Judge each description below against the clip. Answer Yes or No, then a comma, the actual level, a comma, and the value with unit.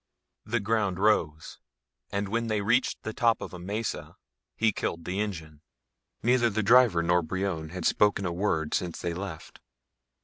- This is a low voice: Yes, low, 100 Hz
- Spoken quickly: No, average, 165 wpm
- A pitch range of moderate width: Yes, average, 4.2 semitones